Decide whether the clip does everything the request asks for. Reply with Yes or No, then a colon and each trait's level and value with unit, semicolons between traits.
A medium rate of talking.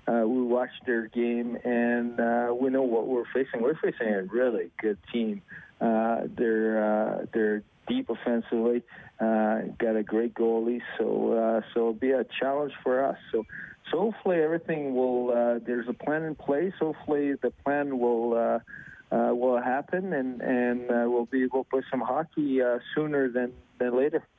Yes: average, 175 wpm